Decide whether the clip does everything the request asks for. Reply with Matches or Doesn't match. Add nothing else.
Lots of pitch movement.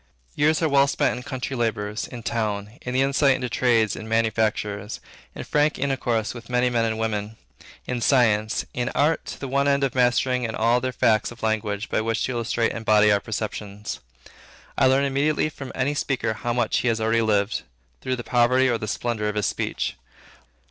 Doesn't match